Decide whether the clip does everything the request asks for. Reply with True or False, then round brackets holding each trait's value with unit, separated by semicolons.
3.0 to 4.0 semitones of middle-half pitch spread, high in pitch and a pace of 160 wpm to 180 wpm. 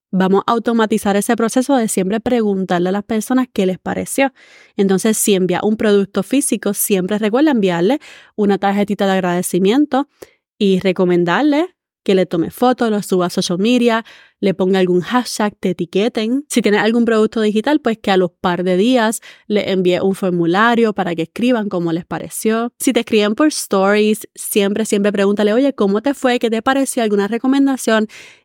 True (3.7 semitones; 210 Hz; 175 wpm)